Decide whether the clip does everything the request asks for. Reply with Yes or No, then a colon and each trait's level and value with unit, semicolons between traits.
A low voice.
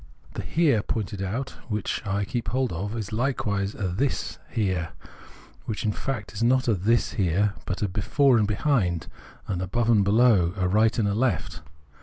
Yes: low, 105 Hz